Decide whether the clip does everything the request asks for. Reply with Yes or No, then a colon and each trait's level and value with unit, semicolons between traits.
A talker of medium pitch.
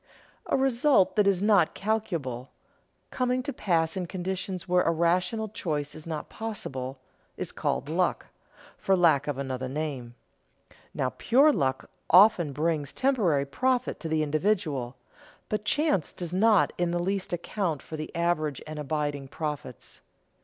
Yes: medium, 170 Hz